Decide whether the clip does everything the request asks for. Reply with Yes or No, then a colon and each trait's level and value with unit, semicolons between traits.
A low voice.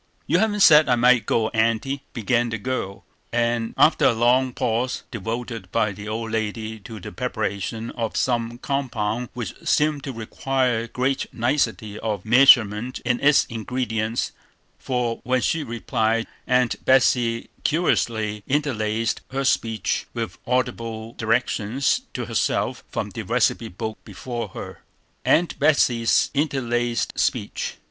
Yes: low, 120 Hz